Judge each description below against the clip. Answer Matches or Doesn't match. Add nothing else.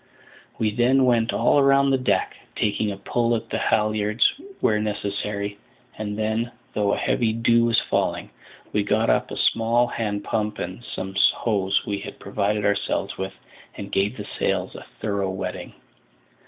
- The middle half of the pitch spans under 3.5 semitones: Matches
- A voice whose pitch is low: Matches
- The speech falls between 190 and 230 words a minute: Doesn't match